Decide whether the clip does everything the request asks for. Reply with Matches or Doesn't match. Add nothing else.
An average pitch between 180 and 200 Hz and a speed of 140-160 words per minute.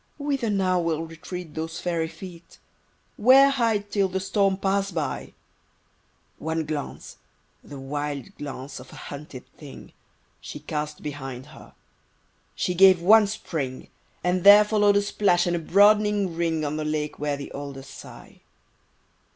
Doesn't match